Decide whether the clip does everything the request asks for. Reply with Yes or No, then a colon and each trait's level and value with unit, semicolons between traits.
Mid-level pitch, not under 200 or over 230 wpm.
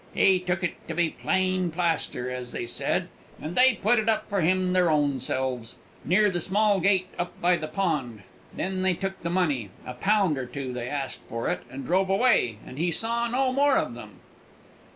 Yes: medium, 175 Hz; fast, 205 wpm